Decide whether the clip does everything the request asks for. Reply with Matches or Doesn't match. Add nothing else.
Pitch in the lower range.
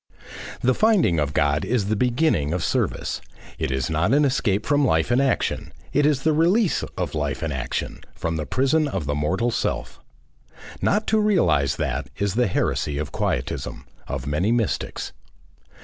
Matches